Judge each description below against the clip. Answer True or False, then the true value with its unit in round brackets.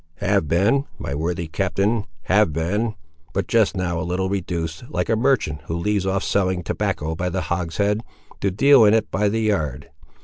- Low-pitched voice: True (95 Hz)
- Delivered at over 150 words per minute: True (175 wpm)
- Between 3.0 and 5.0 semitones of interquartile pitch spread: True (3.8 semitones)